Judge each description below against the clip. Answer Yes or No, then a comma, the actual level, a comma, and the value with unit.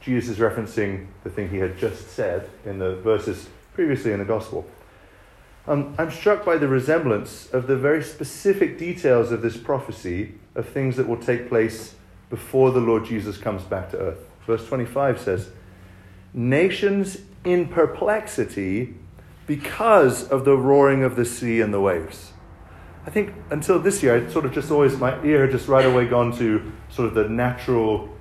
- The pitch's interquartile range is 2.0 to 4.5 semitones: No, average, 4.9 semitones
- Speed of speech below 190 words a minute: Yes, average, 175 wpm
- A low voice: Yes, low, 120 Hz